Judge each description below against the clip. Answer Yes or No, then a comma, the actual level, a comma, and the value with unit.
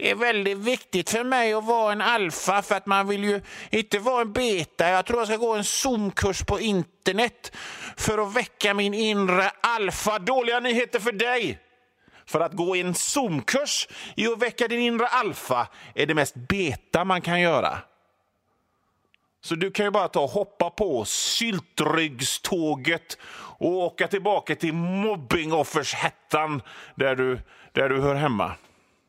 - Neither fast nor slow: Yes, average, 160 wpm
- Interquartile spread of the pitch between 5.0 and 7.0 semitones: Yes, wide, 5.5 semitones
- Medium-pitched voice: No, high, 200 Hz